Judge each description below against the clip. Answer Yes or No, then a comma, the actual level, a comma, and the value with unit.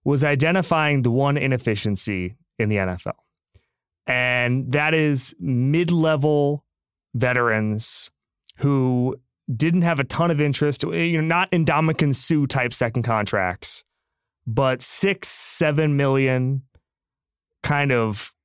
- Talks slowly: Yes, slow, 115 wpm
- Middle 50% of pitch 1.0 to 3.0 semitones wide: No, average, 4.1 semitones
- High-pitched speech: No, low, 135 Hz